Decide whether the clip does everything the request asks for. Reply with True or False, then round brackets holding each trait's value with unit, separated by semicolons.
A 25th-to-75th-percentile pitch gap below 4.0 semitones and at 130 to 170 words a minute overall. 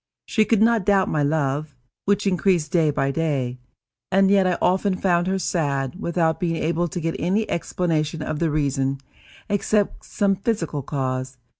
False (4.7 semitones; 165 wpm)